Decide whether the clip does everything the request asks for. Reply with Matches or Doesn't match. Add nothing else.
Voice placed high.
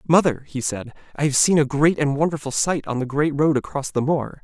Doesn't match